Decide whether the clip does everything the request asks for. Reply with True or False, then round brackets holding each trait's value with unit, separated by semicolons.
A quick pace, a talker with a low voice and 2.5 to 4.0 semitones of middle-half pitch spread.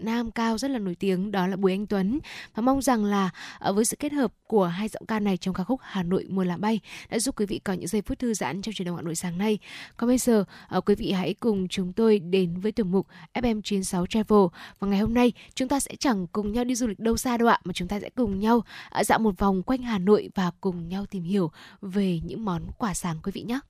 False (270 wpm; 205 Hz; 3.5 semitones)